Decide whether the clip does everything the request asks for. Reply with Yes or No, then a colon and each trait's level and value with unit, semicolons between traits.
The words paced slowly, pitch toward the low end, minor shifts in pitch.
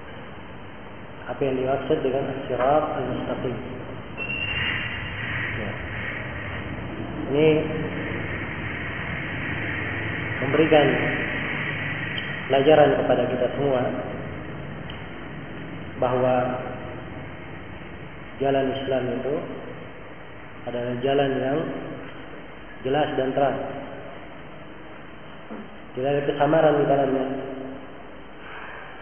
Yes: slow, 60 wpm; low, 130 Hz; narrow, 2.1 semitones